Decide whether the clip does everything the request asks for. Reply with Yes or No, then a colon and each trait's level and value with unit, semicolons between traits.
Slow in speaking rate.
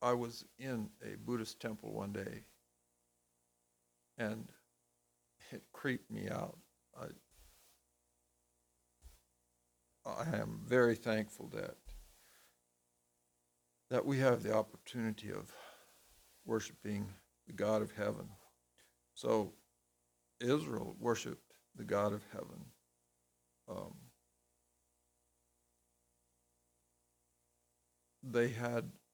Yes: slow, 80 wpm